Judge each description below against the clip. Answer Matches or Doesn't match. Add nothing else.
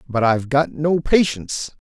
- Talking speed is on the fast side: Doesn't match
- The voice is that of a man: Matches